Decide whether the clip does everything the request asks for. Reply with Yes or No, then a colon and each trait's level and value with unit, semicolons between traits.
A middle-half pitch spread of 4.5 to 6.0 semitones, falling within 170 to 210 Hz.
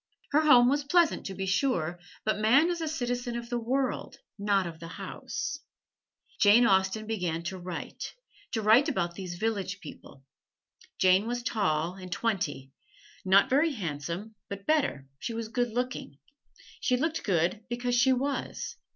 No: average, 5.2 semitones; high, 220 Hz